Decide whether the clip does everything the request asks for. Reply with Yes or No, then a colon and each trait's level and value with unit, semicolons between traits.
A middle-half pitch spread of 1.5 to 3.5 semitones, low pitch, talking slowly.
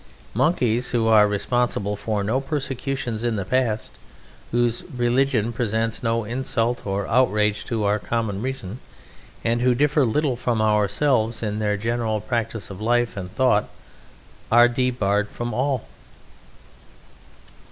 Yes: average, 2.8 semitones; low, 115 Hz; slow, 130 wpm